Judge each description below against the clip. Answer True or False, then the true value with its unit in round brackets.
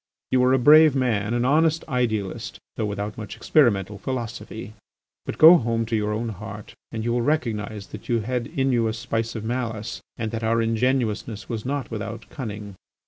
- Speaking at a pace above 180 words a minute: True (190 wpm)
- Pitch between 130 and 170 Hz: False (115 Hz)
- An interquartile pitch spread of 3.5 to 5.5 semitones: False (2.9 semitones)